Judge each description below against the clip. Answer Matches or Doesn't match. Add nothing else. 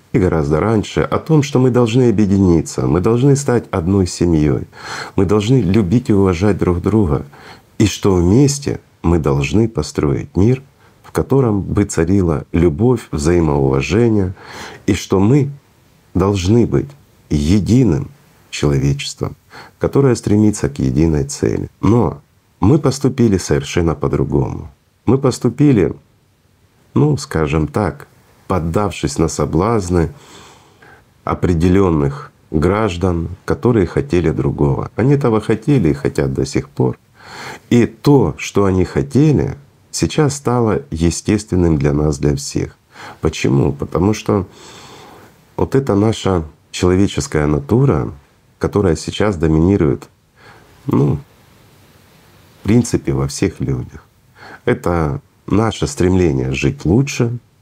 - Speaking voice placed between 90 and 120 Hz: Matches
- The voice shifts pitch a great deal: Matches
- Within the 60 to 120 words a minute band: Matches